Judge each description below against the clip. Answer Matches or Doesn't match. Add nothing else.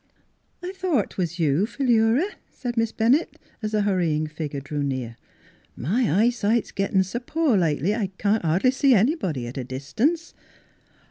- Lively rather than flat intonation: Matches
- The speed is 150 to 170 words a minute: Matches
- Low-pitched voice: Doesn't match